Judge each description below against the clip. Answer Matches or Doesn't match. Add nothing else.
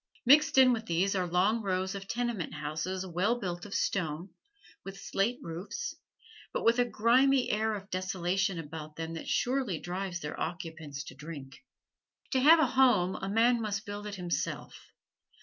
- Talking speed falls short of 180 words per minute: Matches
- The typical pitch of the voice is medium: Doesn't match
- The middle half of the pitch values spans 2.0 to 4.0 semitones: Doesn't match